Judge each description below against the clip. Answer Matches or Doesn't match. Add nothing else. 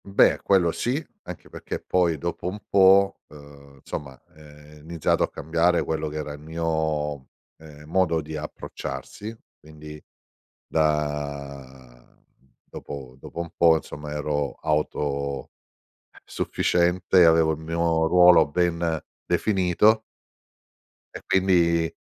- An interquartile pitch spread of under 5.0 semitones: Matches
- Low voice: Matches